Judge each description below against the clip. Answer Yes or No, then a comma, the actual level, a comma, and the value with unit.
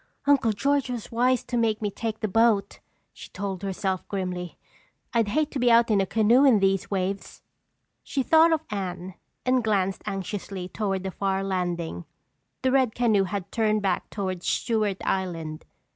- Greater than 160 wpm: Yes, average, 170 wpm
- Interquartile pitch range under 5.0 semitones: Yes, average, 3.7 semitones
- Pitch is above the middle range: Yes, high, 205 Hz